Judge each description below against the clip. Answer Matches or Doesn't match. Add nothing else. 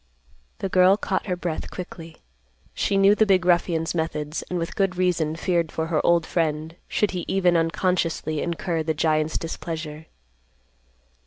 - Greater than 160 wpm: Doesn't match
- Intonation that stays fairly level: Matches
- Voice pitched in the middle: Matches